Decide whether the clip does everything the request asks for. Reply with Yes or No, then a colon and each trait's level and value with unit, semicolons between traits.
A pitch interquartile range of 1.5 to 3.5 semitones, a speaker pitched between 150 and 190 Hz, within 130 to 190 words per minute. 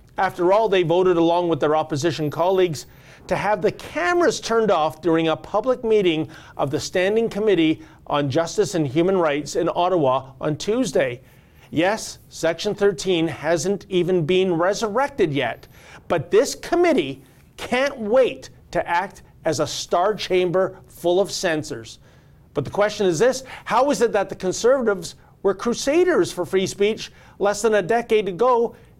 No: average, 5.2 semitones; medium, 185 Hz; average, 155 wpm